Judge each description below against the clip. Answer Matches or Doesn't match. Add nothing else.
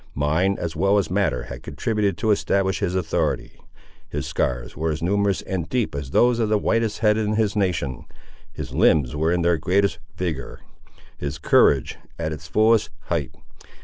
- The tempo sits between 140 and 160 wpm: Doesn't match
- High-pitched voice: Doesn't match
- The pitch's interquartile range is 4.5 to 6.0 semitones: Matches